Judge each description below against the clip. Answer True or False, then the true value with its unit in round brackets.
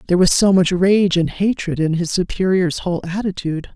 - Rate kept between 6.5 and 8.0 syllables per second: False (5.7 syllables/s)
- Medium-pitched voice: True (180 Hz)